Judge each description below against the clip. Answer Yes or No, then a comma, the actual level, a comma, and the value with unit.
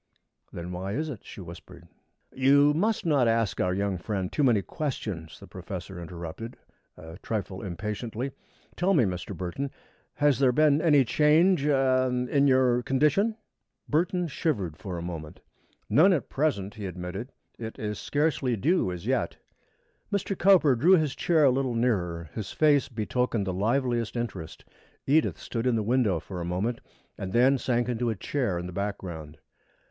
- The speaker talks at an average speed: Yes, average, 165 wpm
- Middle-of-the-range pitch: No, low, 120 Hz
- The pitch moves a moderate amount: No, wide, 7.0 semitones